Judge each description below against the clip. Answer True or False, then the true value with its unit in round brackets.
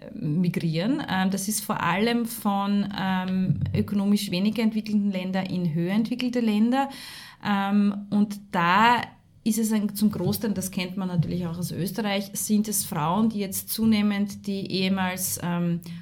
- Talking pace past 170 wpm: False (140 wpm)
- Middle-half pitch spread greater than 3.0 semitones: False (2.7 semitones)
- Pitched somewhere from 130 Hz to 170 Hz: False (200 Hz)